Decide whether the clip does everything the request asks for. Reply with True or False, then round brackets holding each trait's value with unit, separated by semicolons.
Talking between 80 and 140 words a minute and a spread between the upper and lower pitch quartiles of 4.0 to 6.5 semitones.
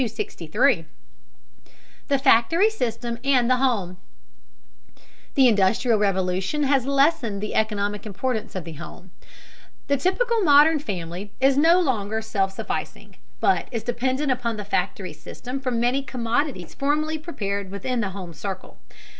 True (135 wpm; 5.6 semitones)